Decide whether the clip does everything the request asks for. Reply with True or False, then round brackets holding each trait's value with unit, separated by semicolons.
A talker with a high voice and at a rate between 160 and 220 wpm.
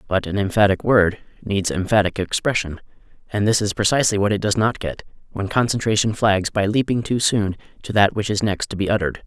False (105 Hz; 200 wpm)